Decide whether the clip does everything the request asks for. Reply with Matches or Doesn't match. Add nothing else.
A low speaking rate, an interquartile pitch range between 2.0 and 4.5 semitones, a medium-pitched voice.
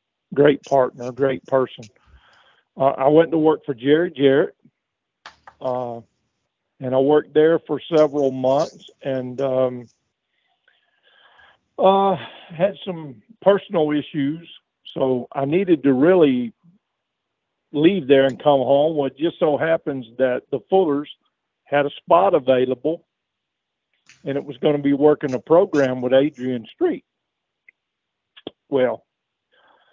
Matches